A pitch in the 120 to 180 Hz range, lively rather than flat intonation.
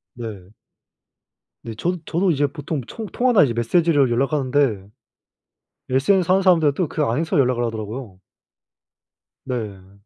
Yes: low, 135 Hz; wide, 6.2 semitones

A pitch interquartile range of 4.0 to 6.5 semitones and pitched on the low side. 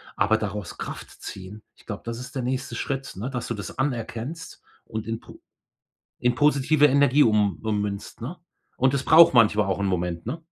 Yes: average, 4.4 semitones; low, 115 Hz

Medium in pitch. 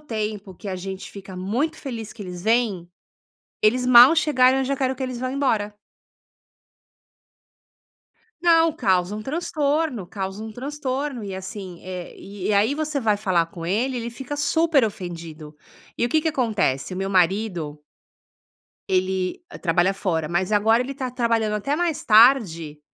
No: high, 215 Hz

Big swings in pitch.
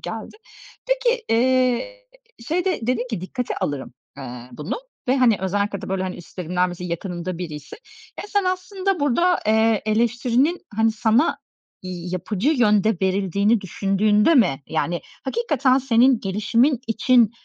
Yes: wide, 6.1 semitones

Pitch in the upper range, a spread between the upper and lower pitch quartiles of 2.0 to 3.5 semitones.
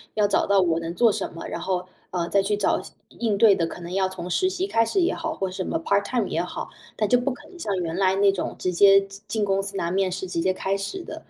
Yes: high, 195 Hz; average, 2.7 semitones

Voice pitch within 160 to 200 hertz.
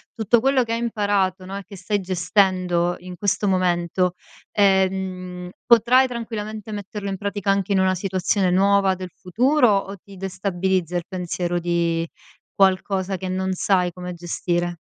Yes: high, 190 Hz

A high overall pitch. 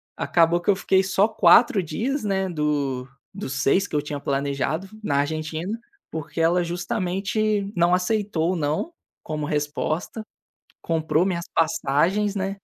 No: medium, 175 Hz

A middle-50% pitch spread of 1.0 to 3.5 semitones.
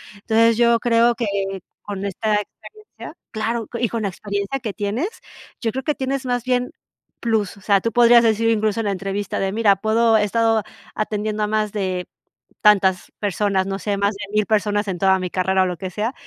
Yes: narrow, 2.5 semitones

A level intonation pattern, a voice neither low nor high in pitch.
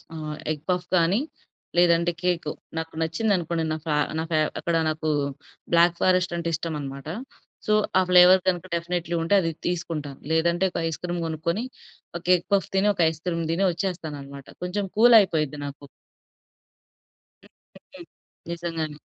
Yes: narrow, 2.2 semitones; medium, 170 Hz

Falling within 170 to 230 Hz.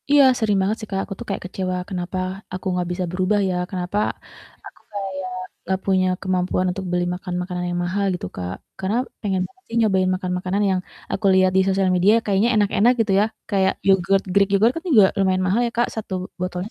Yes: high, 190 Hz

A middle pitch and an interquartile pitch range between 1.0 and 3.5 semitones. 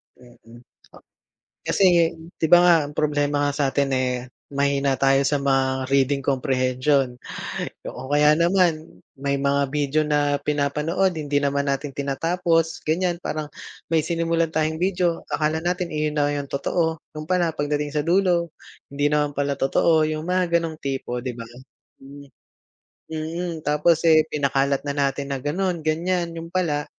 Yes: medium, 150 Hz; average, 3.0 semitones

